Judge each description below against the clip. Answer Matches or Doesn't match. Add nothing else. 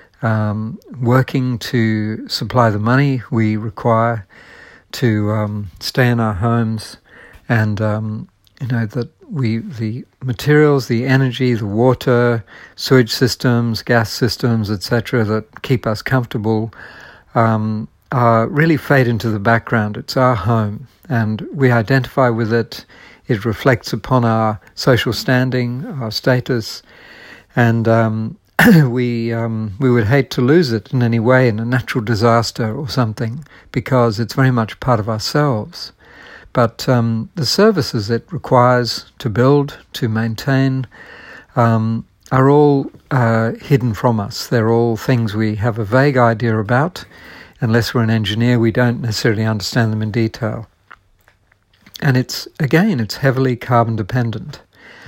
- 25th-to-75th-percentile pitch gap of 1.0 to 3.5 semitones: Matches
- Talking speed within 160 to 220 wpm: Doesn't match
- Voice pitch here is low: Matches